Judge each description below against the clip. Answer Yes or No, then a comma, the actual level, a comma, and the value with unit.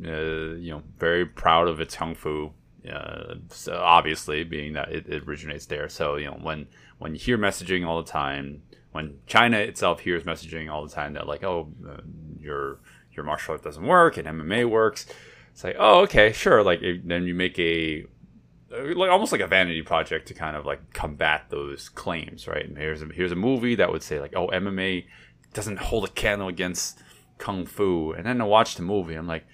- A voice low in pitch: Yes, very low, 80 Hz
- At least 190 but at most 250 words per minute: Yes, fast, 205 wpm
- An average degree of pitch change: Yes, average, 3.3 semitones